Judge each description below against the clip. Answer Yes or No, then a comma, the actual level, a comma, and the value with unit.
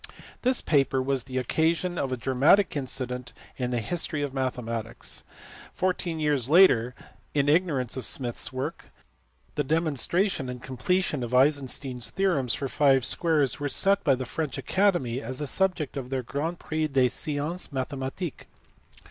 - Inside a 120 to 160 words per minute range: Yes, average, 155 wpm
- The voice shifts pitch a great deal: No, average, 4.0 semitones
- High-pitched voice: No, medium, 140 Hz